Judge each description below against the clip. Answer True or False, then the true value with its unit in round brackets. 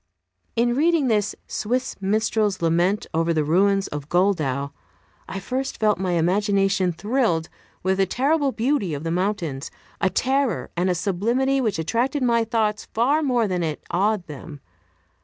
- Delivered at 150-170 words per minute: True (155 wpm)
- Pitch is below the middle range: False (200 Hz)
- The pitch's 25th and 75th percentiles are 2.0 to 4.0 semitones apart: False (5.5 semitones)